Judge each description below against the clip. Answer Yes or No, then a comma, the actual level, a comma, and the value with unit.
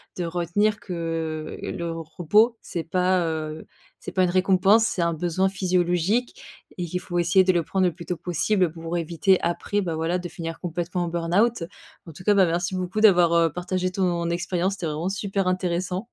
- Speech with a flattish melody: Yes, narrow, 1.9 semitones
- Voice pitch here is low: No, medium, 175 Hz